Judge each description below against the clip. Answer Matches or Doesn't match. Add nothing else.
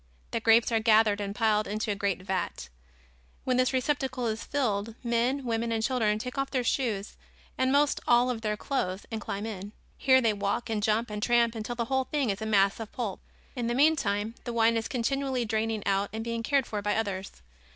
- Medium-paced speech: Doesn't match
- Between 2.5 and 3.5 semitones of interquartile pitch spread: Matches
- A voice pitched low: Doesn't match